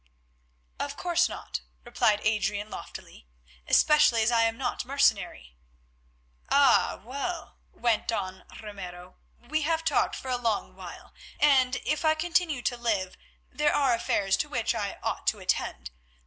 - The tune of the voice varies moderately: No, wide, 5.9 semitones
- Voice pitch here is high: Yes, high, 240 Hz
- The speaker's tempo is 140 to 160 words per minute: Yes, average, 145 wpm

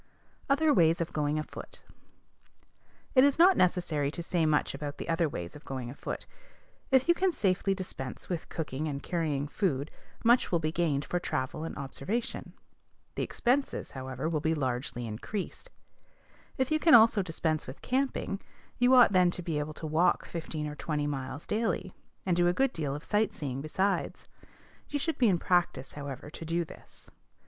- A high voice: No, medium, 165 Hz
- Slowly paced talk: No, average, 180 wpm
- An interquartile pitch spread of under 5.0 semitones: No, wide, 5.6 semitones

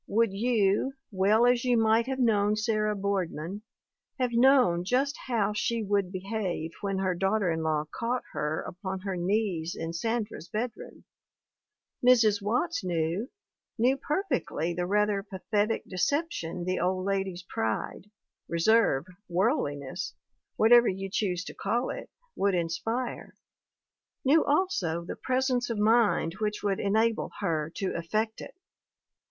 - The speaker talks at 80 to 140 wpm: Yes, slow, 135 wpm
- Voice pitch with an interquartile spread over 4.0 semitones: Yes, average, 4.4 semitones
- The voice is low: No, high, 205 Hz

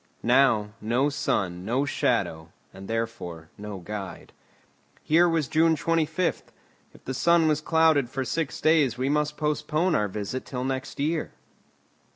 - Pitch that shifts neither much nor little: No, wide, 6.2 semitones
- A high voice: No, low, 135 Hz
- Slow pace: No, average, 145 wpm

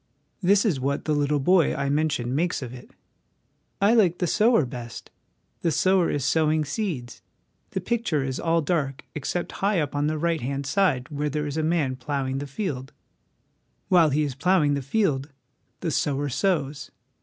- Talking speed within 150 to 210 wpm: Yes, average, 180 wpm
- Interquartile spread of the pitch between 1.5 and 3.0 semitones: No, average, 4.2 semitones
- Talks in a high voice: No, medium, 150 Hz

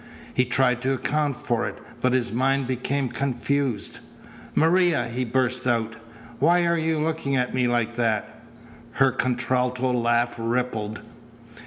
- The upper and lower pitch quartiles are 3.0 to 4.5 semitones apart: No, narrow, 2.5 semitones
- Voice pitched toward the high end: No, low, 125 Hz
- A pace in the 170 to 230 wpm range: No, average, 140 wpm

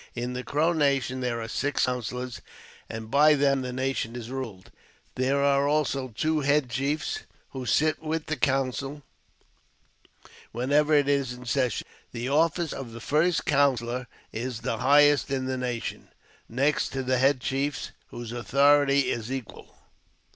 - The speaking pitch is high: No, low, 135 Hz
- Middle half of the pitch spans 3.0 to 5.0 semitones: No, narrow, 2.5 semitones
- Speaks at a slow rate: No, average, 155 wpm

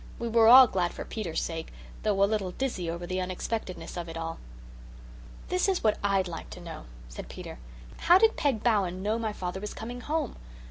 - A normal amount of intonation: Yes, average, 4.7 semitones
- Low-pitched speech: No, high, 200 Hz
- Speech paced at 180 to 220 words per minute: Yes, average, 200 wpm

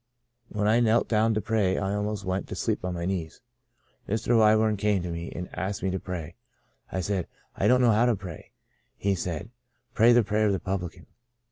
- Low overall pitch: Yes, low, 100 Hz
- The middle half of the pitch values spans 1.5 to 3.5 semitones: Yes, average, 2.9 semitones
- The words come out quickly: Yes, fast, 215 wpm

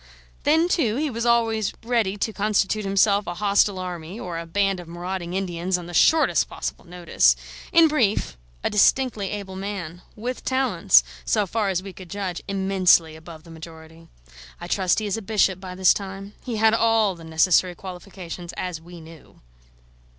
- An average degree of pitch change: Yes, average, 3.5 semitones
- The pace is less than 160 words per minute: No, average, 175 wpm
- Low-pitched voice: No, high, 195 Hz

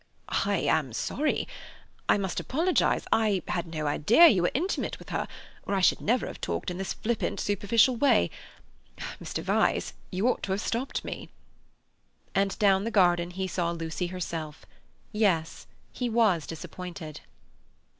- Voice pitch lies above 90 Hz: Yes, high, 190 Hz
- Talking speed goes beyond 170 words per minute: No, average, 155 wpm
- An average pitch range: Yes, average, 4.7 semitones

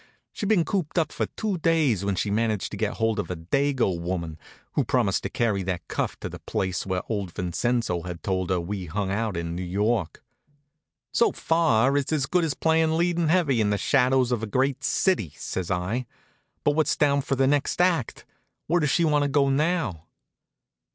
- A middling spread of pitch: No, wide, 8.3 semitones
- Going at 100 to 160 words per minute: No, average, 200 wpm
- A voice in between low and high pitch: No, low, 120 Hz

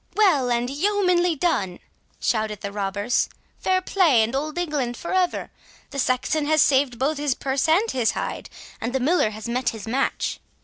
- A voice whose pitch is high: Yes, very high, 270 Hz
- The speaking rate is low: No, average, 175 wpm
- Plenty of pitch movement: Yes, wide, 5.7 semitones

